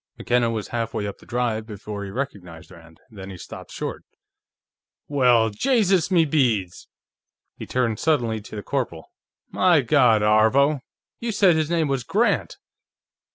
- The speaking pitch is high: No, low, 120 Hz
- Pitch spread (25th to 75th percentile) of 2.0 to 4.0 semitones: No, wide, 5.6 semitones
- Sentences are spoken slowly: No, average, 150 wpm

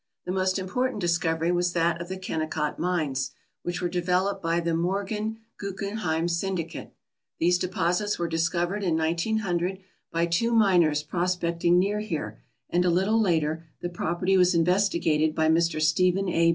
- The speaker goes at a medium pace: Yes, average, 155 wpm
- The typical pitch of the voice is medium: Yes, medium, 175 Hz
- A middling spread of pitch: No, narrow, 2.3 semitones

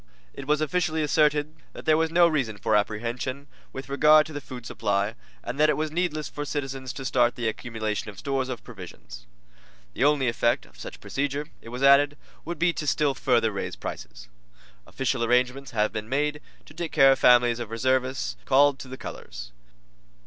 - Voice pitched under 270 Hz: Yes, low, 135 Hz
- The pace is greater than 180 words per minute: Yes, average, 190 wpm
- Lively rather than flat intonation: No, average, 4.1 semitones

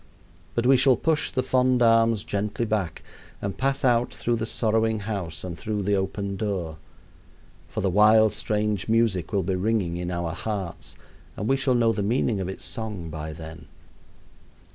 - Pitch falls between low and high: No, low, 105 Hz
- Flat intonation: No, average, 3.5 semitones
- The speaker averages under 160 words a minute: No, average, 175 wpm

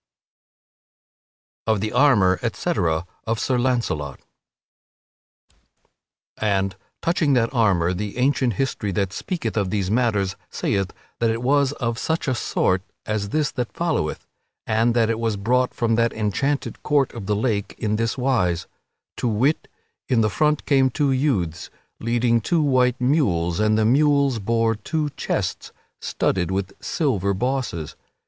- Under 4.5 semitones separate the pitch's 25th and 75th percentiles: No, average, 4.8 semitones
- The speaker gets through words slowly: No, average, 145 wpm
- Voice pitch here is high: No, low, 115 Hz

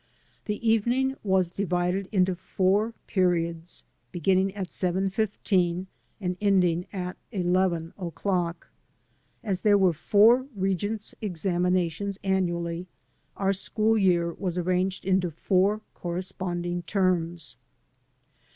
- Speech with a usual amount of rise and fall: No, narrow, 2.1 semitones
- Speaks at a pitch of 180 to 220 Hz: Yes, medium, 185 Hz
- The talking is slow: Yes, slow, 105 wpm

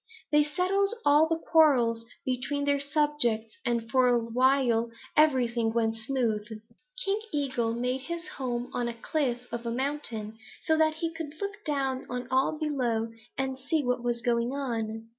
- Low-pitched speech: No, very high, 260 Hz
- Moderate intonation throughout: Yes, average, 4.1 semitones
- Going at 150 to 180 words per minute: Yes, average, 160 wpm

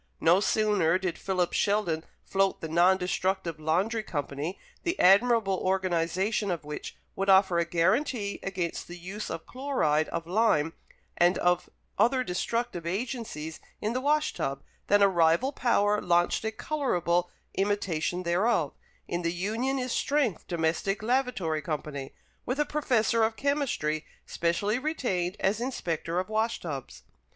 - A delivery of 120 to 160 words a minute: Yes, average, 140 wpm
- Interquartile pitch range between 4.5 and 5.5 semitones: Yes, average, 5.1 semitones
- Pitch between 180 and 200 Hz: Yes, high, 190 Hz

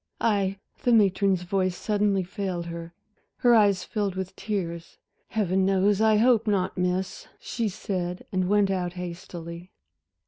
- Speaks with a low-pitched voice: No, high, 190 Hz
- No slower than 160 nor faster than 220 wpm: No, average, 140 wpm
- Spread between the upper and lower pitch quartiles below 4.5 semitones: Yes, narrow, 2.5 semitones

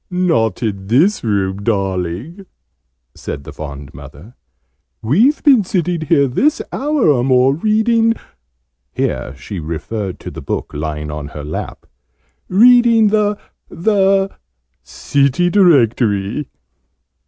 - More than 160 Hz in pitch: No, low, 130 Hz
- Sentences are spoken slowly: Yes, slow, 120 wpm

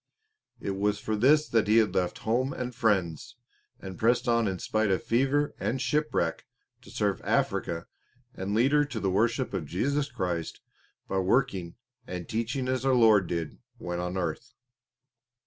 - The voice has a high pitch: No, low, 110 Hz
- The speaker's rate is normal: Yes, average, 165 wpm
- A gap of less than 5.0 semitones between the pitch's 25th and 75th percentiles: No, wide, 5.4 semitones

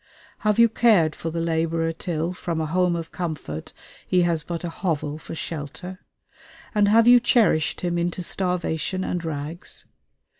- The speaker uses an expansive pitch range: No, narrow, 2.4 semitones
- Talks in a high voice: No, medium, 170 Hz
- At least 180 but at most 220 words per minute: No, average, 160 wpm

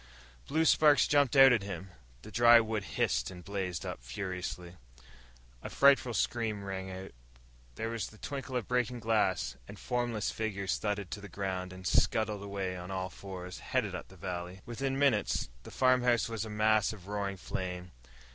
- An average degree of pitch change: Yes, average, 4.1 semitones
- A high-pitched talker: No, low, 100 Hz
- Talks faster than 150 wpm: Yes, average, 170 wpm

